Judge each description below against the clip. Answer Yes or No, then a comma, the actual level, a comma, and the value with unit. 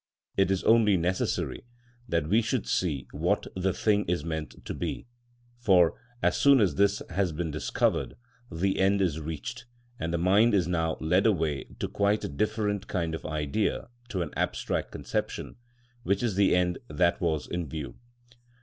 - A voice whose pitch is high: No, very low, 90 Hz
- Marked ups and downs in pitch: No, average, 3.8 semitones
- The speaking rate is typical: Yes, average, 170 wpm